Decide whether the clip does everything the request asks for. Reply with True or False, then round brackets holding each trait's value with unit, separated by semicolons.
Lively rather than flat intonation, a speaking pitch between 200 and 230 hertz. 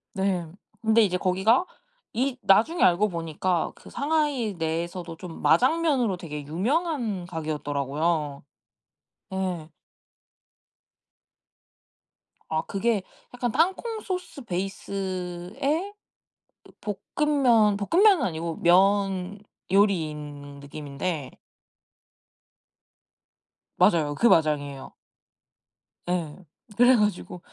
False (6.6 semitones; 190 Hz)